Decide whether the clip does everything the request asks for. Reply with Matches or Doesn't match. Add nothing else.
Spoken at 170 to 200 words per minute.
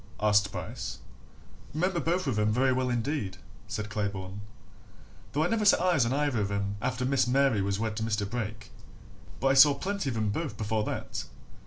Matches